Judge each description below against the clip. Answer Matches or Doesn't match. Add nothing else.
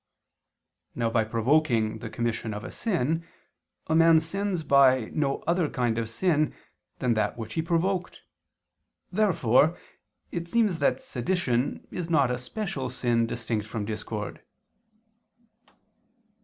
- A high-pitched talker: Doesn't match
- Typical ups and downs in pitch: Doesn't match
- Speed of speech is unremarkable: Doesn't match